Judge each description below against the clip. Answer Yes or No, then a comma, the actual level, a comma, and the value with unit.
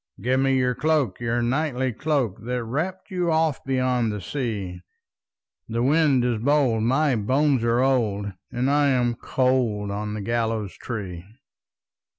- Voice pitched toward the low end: Yes, low, 125 Hz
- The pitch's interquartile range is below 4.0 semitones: Yes, average, 3.6 semitones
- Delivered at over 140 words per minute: Yes, average, 150 wpm